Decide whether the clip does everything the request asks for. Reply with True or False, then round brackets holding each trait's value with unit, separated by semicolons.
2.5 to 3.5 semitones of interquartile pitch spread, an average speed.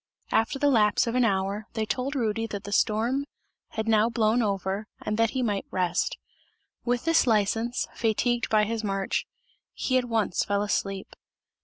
True (2.9 semitones; 170 wpm)